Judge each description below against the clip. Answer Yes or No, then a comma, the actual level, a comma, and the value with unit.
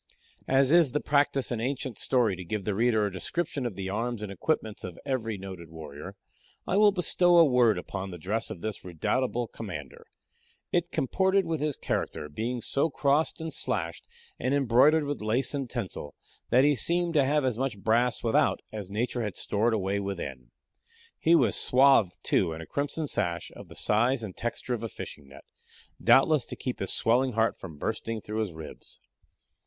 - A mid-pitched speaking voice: No, low, 115 Hz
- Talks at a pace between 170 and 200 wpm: Yes, average, 190 wpm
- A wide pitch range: Yes, wide, 5.9 semitones